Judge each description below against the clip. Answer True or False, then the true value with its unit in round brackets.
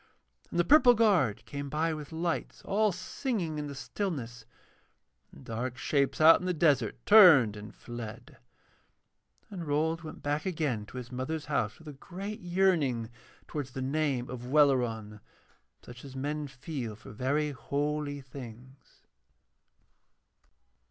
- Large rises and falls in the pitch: False (4.6 semitones)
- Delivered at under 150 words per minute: True (140 wpm)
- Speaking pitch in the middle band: True (145 Hz)